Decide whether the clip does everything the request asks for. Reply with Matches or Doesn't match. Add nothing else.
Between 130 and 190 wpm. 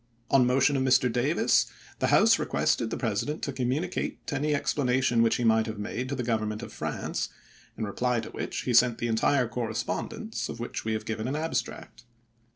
Doesn't match